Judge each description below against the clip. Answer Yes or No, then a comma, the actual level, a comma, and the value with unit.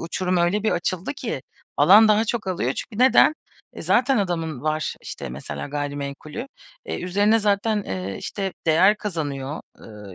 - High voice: No, medium, 180 Hz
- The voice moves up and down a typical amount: No, wide, 6.4 semitones